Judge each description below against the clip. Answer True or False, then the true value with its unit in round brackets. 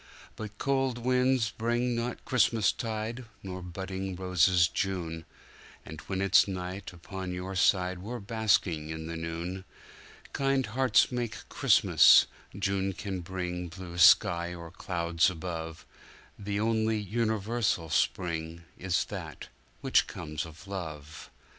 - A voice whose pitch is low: True (95 Hz)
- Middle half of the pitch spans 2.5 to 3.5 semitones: False (4.3 semitones)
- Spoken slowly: True (110 wpm)